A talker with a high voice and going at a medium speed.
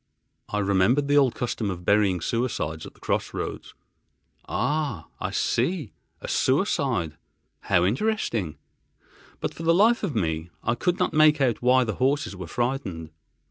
No: low, 120 Hz; average, 150 wpm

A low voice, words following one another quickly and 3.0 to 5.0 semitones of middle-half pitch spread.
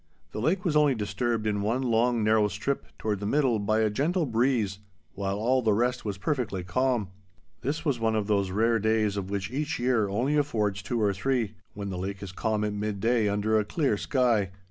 Yes: low, 110 Hz; fast, 210 wpm; average, 3.5 semitones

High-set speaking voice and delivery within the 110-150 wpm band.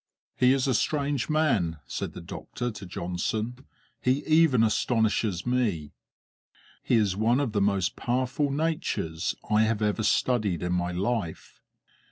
No: low, 110 Hz; average, 145 wpm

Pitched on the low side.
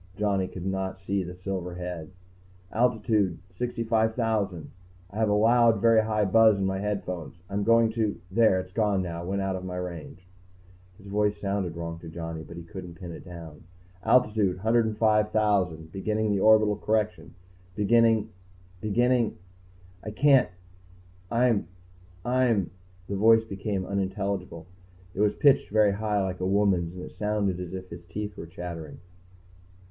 Yes: low, 100 Hz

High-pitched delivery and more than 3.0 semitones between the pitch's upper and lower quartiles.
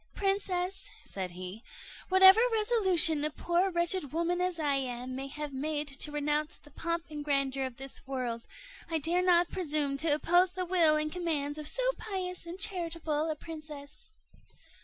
Yes: very high, 310 Hz; average, 4.0 semitones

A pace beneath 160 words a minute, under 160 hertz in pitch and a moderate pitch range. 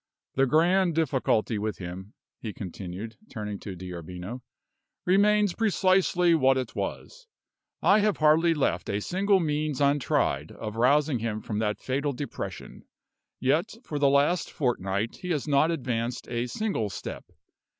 No: average, 140 wpm; low, 135 Hz; wide, 7.5 semitones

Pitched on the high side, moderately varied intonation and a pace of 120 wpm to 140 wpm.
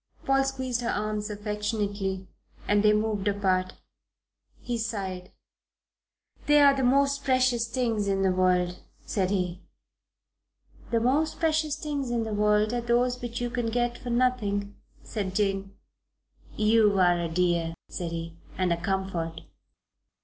Yes: high, 210 Hz; average, 4.2 semitones; slow, 135 wpm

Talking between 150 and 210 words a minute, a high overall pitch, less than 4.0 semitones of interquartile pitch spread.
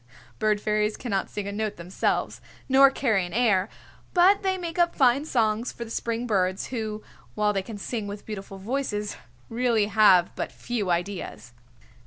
Yes: average, 170 wpm; high, 215 Hz; average, 3.4 semitones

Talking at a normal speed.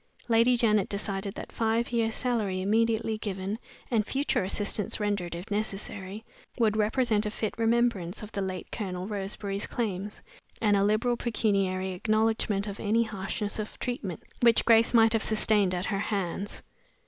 Yes: average, 155 wpm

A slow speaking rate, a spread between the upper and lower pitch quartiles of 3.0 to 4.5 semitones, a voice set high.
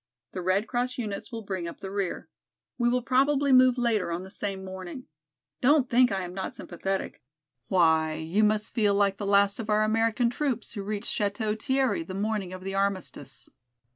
No: average, 190 wpm; average, 3.9 semitones; high, 205 Hz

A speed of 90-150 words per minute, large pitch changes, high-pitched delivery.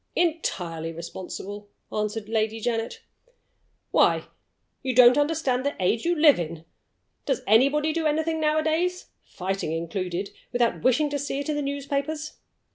Yes: slow, 135 wpm; wide, 6.9 semitones; very high, 255 Hz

